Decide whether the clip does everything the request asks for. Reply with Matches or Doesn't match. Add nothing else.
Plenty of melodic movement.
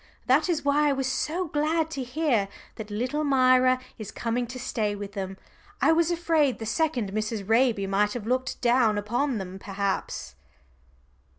Matches